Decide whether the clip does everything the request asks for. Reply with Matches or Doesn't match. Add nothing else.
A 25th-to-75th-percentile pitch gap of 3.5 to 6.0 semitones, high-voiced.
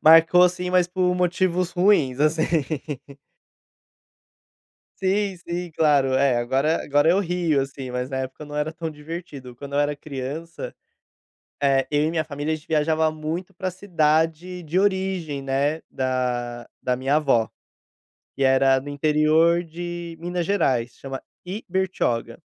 Doesn't match